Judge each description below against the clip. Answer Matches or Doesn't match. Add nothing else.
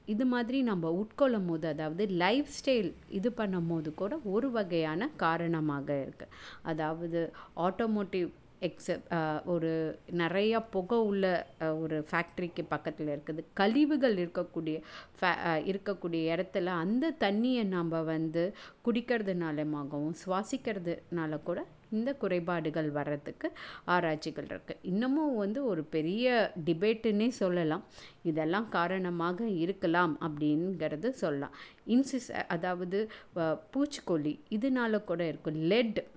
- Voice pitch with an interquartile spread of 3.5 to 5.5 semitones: Matches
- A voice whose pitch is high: Doesn't match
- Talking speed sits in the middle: Matches